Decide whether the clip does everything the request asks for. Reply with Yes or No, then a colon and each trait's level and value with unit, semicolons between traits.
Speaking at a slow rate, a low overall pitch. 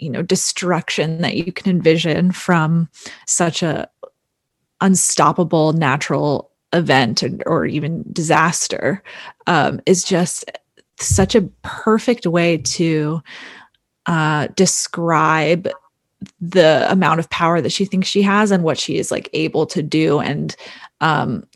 No: slow, 130 wpm; medium, 170 Hz